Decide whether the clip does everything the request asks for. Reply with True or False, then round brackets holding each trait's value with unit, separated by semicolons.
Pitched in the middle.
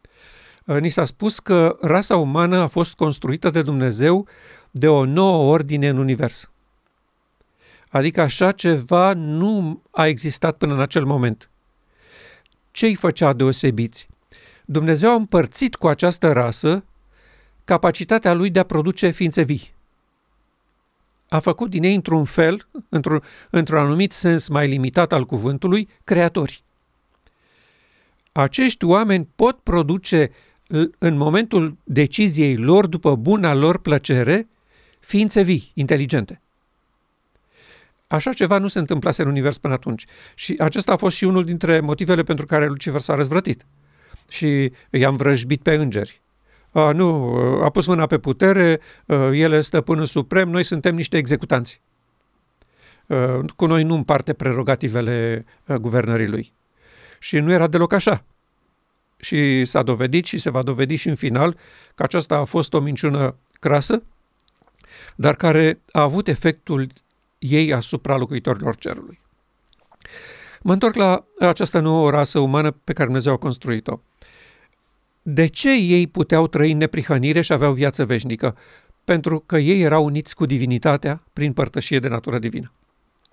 True (155 Hz)